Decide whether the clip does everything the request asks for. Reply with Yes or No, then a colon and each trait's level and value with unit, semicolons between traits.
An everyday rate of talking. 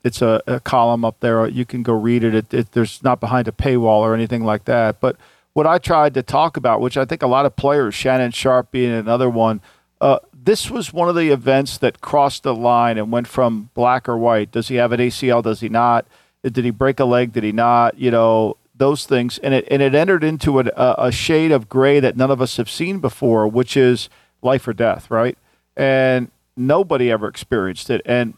No: fast, 230 wpm